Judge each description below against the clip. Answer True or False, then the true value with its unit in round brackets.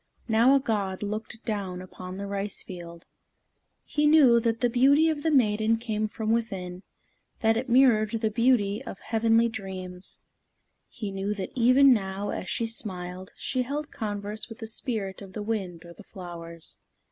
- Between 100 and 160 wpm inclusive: False (170 wpm)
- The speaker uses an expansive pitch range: False (3.5 semitones)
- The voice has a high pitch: True (215 Hz)